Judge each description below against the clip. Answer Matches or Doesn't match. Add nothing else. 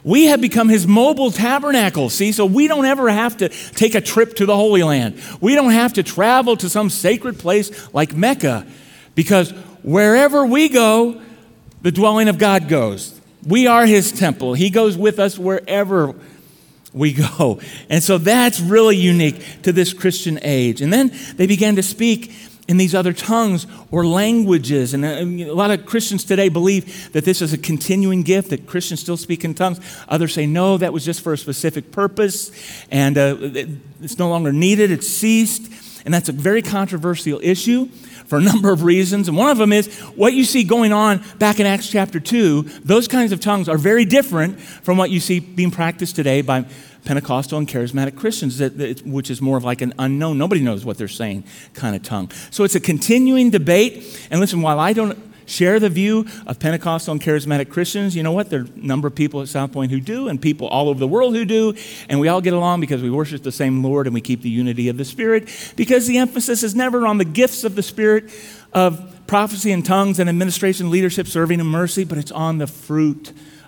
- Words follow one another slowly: Doesn't match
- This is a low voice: Doesn't match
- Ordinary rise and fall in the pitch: Doesn't match